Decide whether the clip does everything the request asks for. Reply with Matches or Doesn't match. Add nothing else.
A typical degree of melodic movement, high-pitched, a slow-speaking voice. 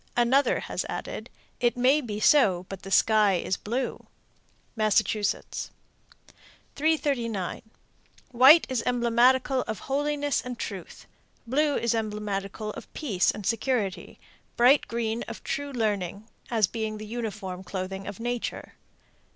Matches